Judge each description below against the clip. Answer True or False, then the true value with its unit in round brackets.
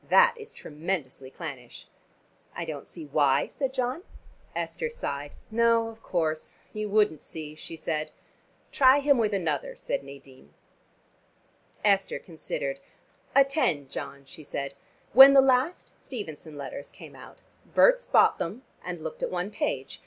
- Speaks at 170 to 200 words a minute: False (140 wpm)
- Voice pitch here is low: False (180 Hz)